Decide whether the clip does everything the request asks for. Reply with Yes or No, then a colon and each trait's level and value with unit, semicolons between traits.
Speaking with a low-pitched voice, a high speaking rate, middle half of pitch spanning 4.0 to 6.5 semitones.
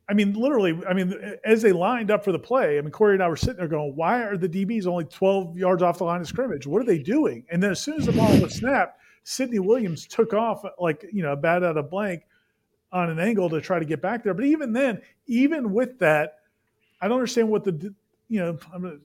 No: high, 190 Hz; fast, 260 wpm; average, 4.6 semitones